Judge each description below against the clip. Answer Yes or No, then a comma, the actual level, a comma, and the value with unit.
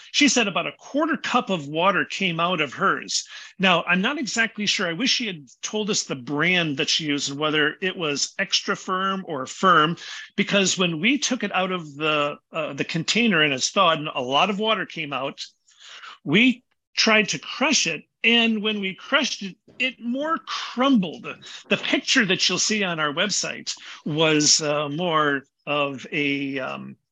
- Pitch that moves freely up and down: Yes, wide, 6.4 semitones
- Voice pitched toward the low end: No, medium, 185 Hz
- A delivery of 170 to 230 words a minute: Yes, average, 185 wpm